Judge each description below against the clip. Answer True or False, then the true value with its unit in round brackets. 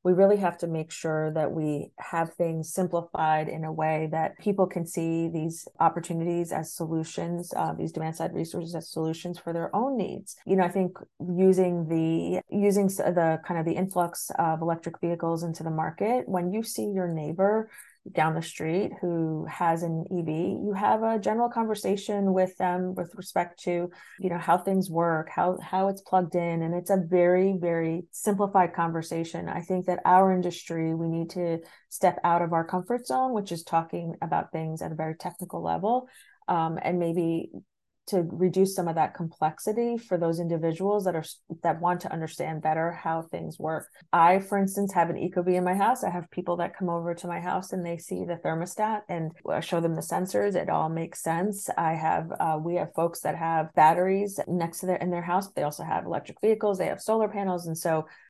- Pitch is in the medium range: True (175 Hz)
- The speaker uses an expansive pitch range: False (2.3 semitones)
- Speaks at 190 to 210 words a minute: True (200 wpm)